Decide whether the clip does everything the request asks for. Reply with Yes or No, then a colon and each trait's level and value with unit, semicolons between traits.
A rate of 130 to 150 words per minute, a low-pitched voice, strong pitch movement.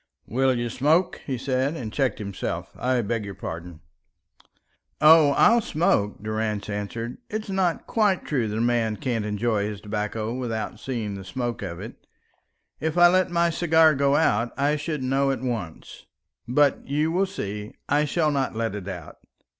No: average, 170 wpm; low, 125 Hz; wide, 6.2 semitones